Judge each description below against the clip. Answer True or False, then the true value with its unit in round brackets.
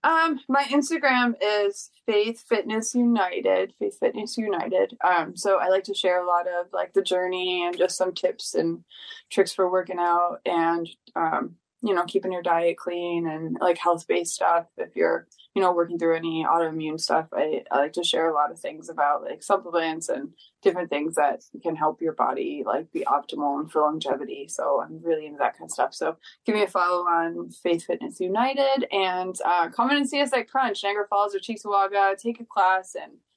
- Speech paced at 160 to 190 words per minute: False (200 wpm)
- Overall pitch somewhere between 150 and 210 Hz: True (185 Hz)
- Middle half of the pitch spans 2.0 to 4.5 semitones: False (5.2 semitones)